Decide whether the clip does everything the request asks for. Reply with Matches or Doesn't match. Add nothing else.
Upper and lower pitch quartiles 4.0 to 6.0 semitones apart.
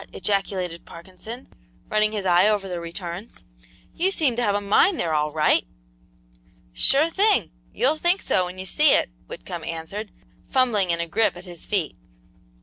Matches